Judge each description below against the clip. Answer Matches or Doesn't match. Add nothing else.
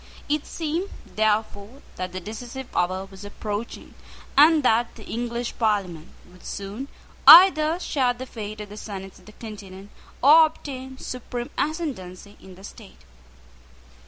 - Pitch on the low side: Doesn't match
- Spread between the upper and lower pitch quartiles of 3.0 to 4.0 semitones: Doesn't match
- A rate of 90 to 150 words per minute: Matches